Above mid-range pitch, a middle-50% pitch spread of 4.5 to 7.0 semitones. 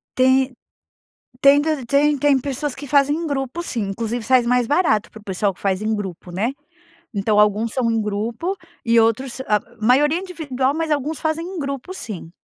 Yes: very high, 260 Hz; average, 5.0 semitones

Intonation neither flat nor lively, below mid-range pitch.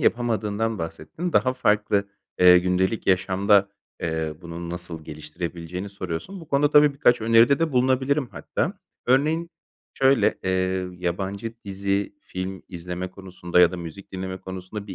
Yes: average, 4.5 semitones; very low, 95 Hz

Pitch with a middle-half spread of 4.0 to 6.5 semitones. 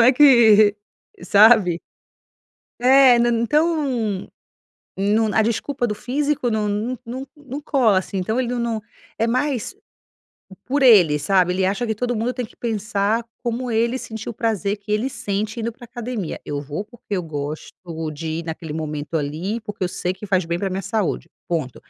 Yes: average, 4.4 semitones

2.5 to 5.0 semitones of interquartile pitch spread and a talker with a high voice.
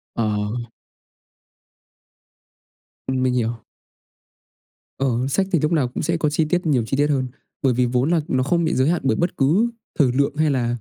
No: average, 4.2 semitones; low, 135 Hz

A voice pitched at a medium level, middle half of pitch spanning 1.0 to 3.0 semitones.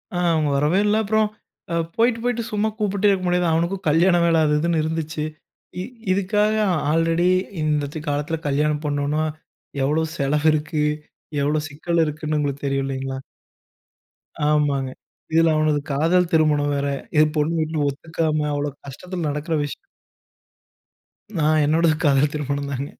Yes: medium, 155 Hz; narrow, 2.6 semitones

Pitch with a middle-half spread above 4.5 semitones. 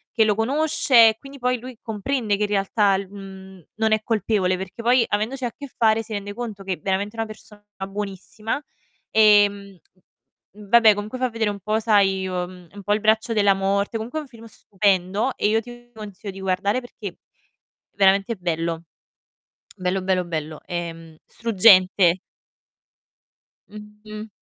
No: average, 2.7 semitones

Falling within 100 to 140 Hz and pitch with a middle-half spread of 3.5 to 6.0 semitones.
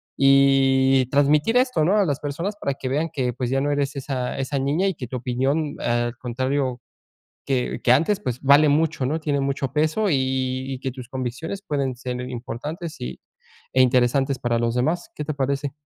No: low, 135 Hz; average, 2.8 semitones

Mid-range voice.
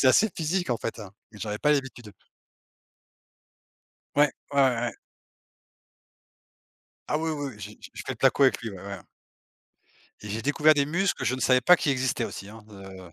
No: low, 130 Hz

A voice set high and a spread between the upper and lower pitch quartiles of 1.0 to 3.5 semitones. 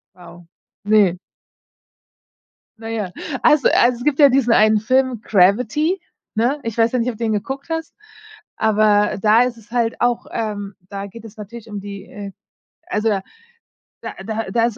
Yes: high, 225 Hz; average, 2.8 semitones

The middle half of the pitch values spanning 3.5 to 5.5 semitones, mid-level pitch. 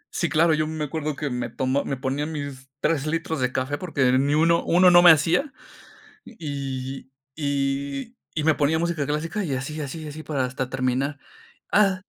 No: average, 3.0 semitones; medium, 145 Hz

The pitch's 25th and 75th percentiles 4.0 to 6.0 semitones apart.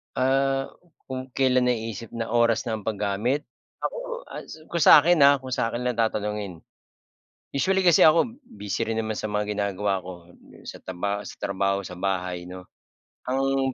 Yes: average, 4.9 semitones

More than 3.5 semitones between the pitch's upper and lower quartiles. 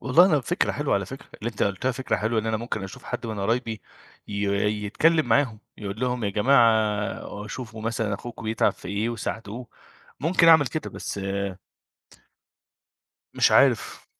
No: average, 3.2 semitones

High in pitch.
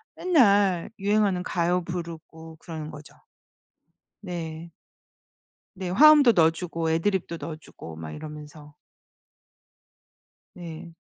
No: medium, 170 Hz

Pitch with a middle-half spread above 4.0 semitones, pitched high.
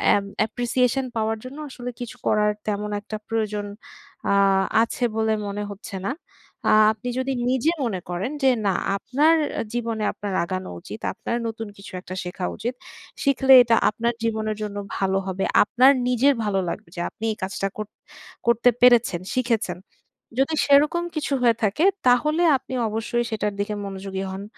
No: average, 3.7 semitones; high, 225 Hz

